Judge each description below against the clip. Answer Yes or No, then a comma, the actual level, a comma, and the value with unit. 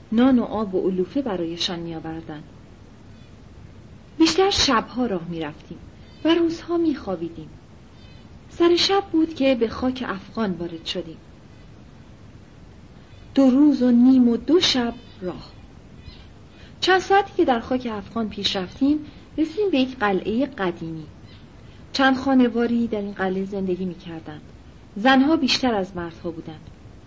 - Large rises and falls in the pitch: Yes, wide, 7.9 semitones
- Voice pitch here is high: Yes, high, 225 Hz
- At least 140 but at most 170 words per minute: No, average, 125 wpm